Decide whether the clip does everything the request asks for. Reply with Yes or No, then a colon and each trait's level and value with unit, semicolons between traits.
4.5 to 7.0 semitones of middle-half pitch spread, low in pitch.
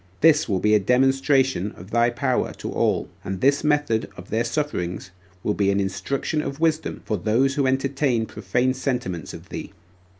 Yes: average, 4.9 semitones; low, 125 Hz